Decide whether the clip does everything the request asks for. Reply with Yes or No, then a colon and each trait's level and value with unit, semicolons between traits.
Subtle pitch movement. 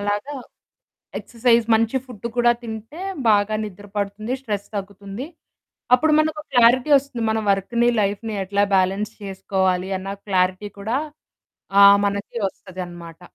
No: average, 3.1 semitones